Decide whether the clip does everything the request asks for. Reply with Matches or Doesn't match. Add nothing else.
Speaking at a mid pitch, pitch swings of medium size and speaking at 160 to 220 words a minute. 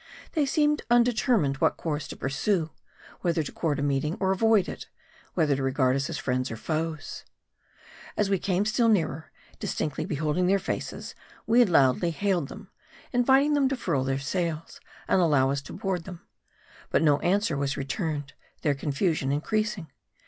Doesn't match